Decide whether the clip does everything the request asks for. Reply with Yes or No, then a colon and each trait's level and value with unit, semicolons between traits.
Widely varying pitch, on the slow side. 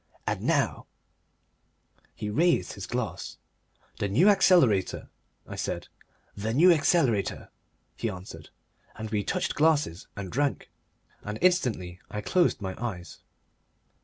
Yes: wide, 8.0 semitones; slow, 125 wpm